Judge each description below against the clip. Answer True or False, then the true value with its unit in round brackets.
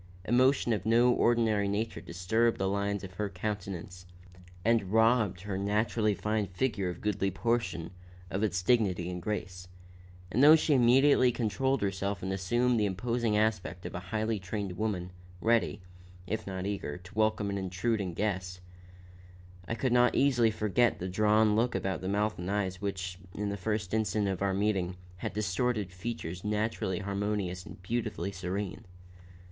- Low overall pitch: True (105 Hz)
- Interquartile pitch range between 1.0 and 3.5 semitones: True (3.2 semitones)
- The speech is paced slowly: False (160 wpm)